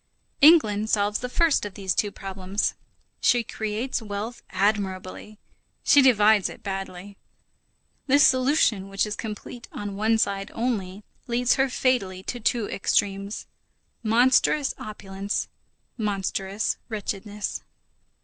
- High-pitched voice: Yes, high, 210 Hz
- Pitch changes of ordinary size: Yes, average, 3.3 semitones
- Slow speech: Yes, slow, 115 wpm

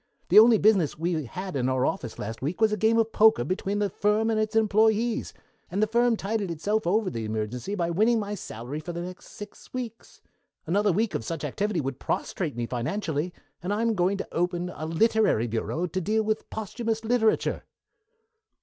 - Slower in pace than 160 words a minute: No, average, 195 wpm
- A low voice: No, high, 195 Hz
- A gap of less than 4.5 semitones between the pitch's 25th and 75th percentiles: No, wide, 5.5 semitones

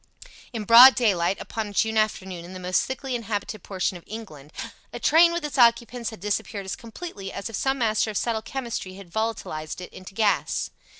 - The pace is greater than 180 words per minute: Yes, average, 195 wpm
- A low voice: No, high, 215 Hz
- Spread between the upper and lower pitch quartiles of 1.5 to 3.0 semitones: No, average, 3.6 semitones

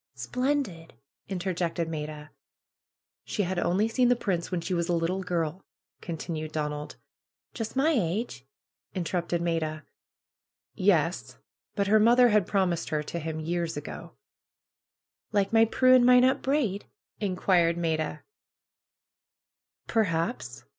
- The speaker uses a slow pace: Yes, slow, 120 wpm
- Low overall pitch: No, medium, 180 Hz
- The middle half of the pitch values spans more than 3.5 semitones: Yes, average, 4.8 semitones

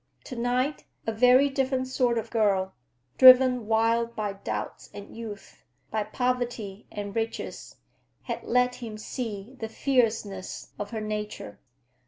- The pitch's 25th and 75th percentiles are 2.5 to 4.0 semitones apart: Yes, average, 3.3 semitones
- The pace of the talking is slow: Yes, slow, 125 wpm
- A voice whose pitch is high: Yes, high, 225 Hz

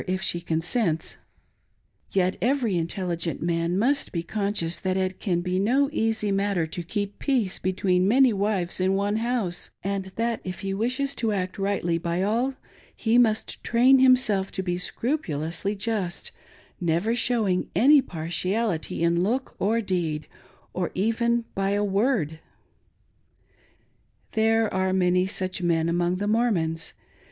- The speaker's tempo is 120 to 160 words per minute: Yes, average, 145 wpm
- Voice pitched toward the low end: No, high, 195 Hz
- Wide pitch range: No, average, 4.3 semitones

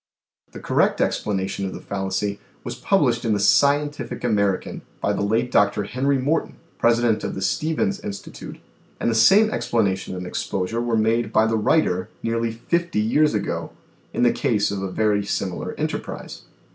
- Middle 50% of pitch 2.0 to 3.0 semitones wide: No, average, 3.8 semitones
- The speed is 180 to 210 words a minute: No, average, 170 wpm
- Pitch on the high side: No, low, 110 Hz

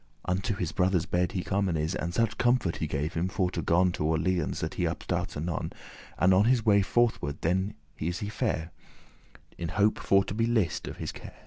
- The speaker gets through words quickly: Yes, fast, 220 wpm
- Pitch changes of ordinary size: Yes, average, 3.5 semitones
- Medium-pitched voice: No, very low, 95 Hz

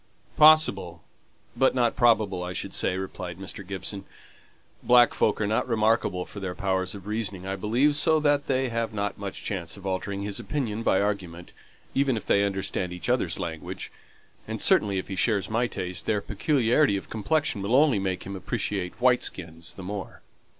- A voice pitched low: Yes, low, 100 Hz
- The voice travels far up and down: No, average, 4.0 semitones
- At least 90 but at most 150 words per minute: No, average, 180 wpm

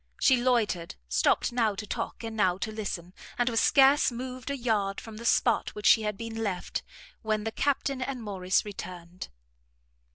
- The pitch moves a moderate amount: Yes, average, 3.7 semitones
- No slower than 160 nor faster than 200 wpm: Yes, average, 180 wpm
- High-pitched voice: Yes, high, 220 Hz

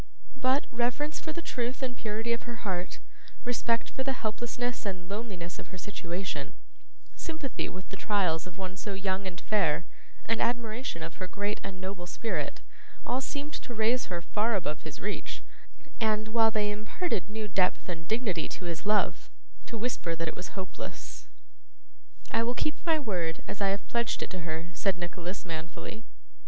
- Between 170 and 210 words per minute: Yes, average, 175 wpm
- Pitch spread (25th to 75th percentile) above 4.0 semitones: Yes, average, 4.7 semitones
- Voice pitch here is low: No, high, 205 Hz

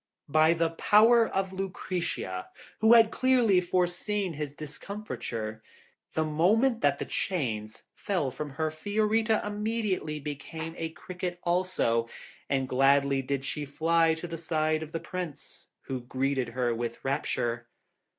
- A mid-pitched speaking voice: Yes, medium, 160 Hz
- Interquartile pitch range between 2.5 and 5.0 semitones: No, wide, 5.6 semitones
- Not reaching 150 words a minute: Yes, slow, 135 wpm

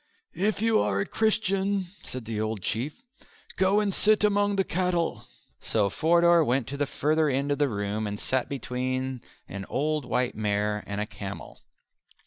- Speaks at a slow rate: No, average, 170 wpm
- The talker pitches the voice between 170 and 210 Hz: No, low, 135 Hz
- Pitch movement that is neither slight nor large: No, wide, 9.0 semitones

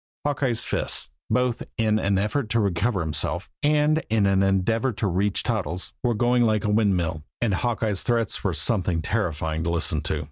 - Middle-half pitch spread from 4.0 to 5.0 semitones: Yes, average, 4.4 semitones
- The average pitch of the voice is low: Yes, low, 105 Hz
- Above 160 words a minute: Yes, average, 175 wpm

